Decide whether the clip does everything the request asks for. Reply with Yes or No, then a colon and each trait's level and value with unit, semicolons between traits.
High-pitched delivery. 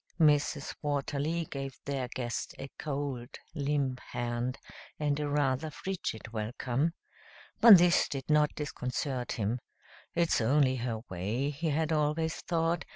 No: medium, 140 Hz